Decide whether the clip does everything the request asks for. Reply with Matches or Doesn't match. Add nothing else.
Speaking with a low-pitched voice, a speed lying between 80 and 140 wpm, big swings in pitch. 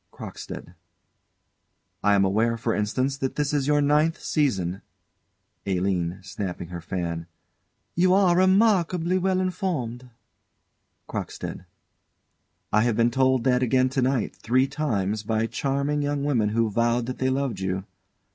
Matches